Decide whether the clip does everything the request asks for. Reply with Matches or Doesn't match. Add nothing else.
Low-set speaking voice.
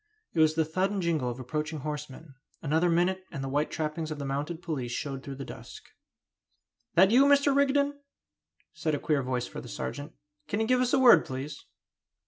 Doesn't match